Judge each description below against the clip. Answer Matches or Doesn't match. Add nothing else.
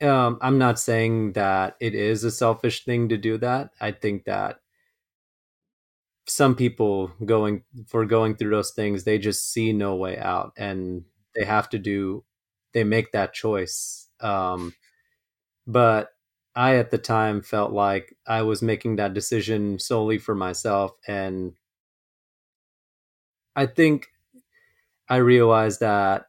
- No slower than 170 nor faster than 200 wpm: Doesn't match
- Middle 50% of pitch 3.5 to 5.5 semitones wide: Doesn't match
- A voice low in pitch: Matches